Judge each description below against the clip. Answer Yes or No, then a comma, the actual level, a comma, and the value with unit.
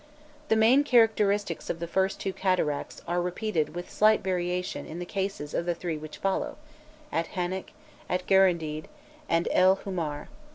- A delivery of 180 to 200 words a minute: No, average, 165 wpm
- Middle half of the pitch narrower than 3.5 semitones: Yes, narrow, 2.6 semitones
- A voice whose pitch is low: No, medium, 180 Hz